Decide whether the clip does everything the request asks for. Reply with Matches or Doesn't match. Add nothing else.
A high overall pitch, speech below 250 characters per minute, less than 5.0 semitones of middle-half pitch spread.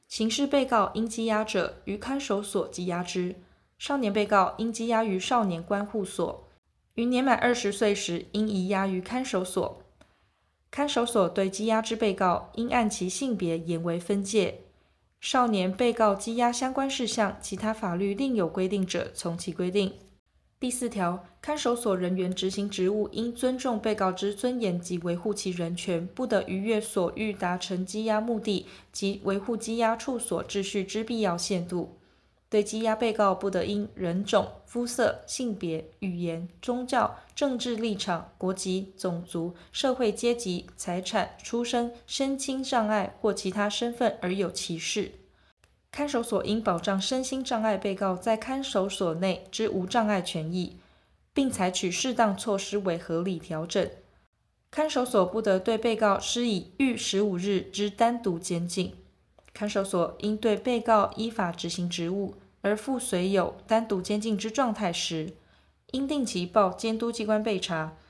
Matches